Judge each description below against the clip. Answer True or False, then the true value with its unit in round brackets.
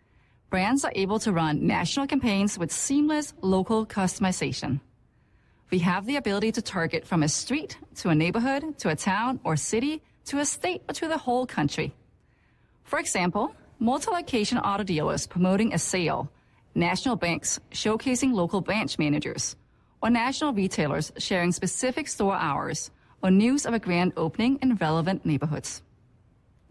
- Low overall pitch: False (190 Hz)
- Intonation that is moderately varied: False (7.8 semitones)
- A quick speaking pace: False (150 wpm)